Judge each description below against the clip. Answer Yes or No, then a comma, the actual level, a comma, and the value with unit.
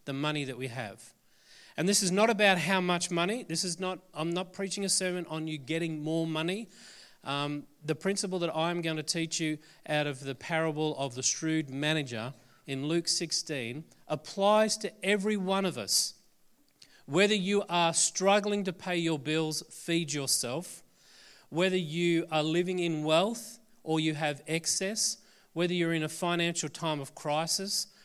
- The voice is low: No, medium, 165 Hz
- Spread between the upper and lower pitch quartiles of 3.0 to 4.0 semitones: Yes, average, 3.5 semitones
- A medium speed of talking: Yes, average, 170 wpm